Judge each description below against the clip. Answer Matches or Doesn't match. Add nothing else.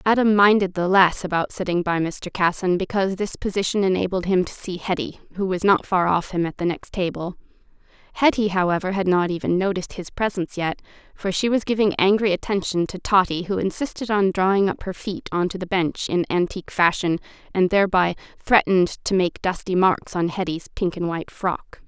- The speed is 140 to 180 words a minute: Doesn't match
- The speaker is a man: Doesn't match